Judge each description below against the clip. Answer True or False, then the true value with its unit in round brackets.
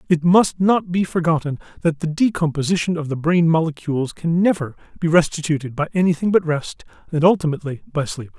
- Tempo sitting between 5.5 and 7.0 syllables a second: True (5.9 syllables/s)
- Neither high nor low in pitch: True (160 Hz)